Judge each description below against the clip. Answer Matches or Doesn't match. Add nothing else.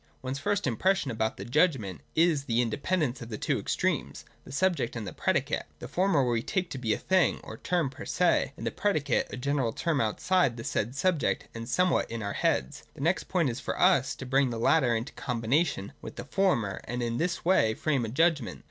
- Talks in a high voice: Doesn't match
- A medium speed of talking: Doesn't match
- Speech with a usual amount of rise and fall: Doesn't match